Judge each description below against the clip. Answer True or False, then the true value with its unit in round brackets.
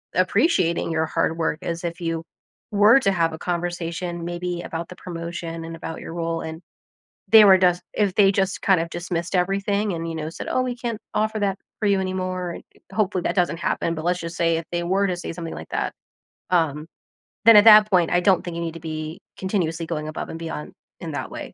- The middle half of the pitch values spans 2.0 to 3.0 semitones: True (2.5 semitones)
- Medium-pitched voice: True (175 Hz)